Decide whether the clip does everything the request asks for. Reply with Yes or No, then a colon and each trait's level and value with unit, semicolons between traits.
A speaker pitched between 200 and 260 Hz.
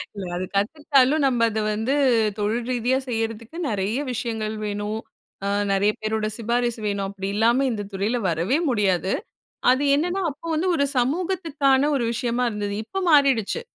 Yes: high, 230 Hz